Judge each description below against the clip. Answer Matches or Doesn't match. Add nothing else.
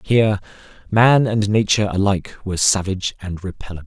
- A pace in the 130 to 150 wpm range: Matches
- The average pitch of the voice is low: Matches